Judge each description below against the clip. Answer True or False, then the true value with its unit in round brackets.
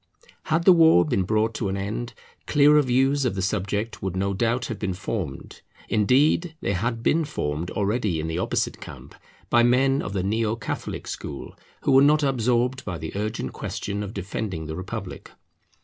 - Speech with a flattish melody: False (5.0 semitones)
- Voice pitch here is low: True (110 Hz)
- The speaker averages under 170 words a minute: False (180 wpm)